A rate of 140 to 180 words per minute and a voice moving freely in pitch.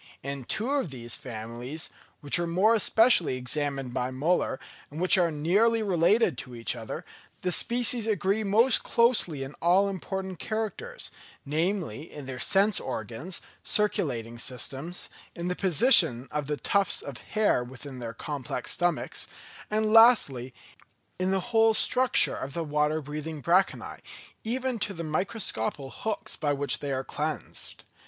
Yes: average, 145 wpm; wide, 7.5 semitones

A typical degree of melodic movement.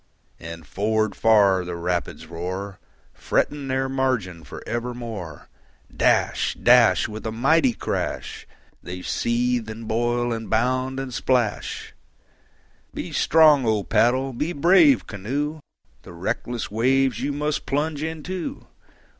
Yes: average, 4.7 semitones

